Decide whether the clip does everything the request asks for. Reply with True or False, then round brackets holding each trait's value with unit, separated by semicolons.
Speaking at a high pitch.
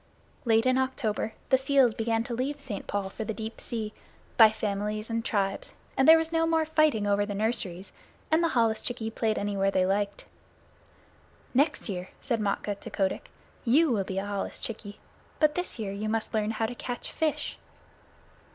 True (220 Hz)